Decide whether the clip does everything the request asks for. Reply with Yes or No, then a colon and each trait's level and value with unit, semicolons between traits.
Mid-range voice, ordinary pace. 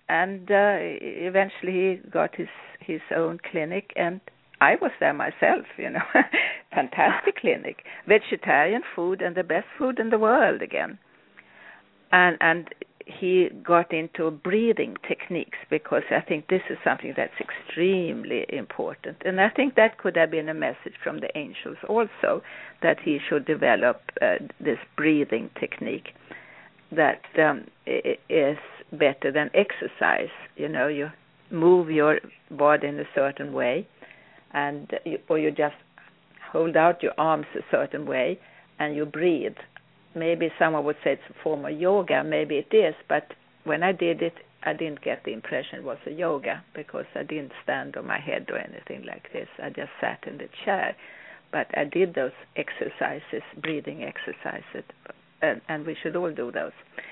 Yes: medium, 170 Hz; average, 160 wpm